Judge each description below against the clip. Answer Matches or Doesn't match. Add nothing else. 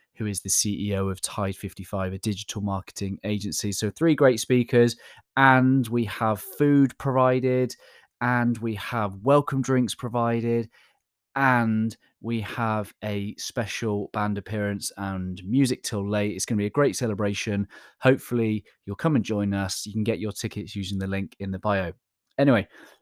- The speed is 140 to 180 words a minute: Matches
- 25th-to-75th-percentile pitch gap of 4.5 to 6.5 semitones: Doesn't match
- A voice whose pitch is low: Matches